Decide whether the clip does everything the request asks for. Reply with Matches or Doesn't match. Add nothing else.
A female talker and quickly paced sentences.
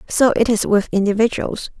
Doesn't match